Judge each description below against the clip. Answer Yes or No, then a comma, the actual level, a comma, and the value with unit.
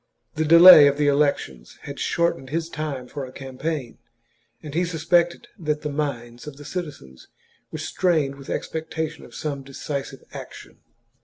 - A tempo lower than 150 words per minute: No, average, 160 wpm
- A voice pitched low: No, medium, 150 Hz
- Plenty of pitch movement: No, average, 2.8 semitones